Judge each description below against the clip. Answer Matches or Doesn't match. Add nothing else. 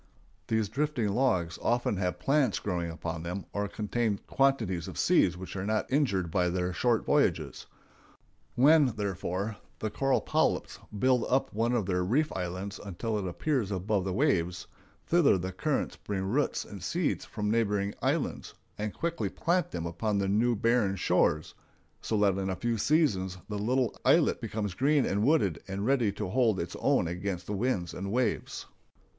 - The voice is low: Matches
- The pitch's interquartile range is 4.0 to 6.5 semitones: Matches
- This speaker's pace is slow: Doesn't match